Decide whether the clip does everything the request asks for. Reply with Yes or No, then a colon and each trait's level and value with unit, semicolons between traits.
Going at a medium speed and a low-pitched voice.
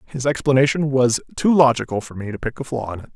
No: fast, 245 wpm; low, 130 Hz